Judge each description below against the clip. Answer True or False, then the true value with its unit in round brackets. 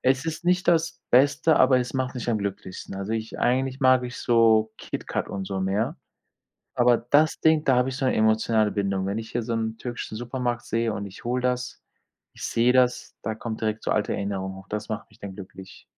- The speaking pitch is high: False (115 Hz)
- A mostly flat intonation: False (3.3 semitones)